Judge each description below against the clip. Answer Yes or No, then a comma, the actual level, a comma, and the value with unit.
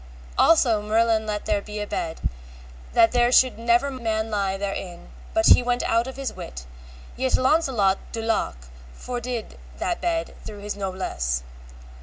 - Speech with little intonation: No, average, 3.6 semitones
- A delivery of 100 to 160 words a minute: Yes, average, 155 wpm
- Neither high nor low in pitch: No, high, 225 Hz